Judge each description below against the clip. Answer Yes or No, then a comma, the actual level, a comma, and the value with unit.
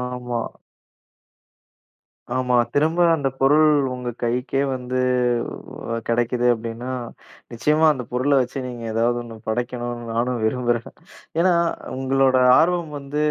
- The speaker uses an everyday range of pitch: No, narrow, 2.2 semitones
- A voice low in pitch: Yes, low, 125 Hz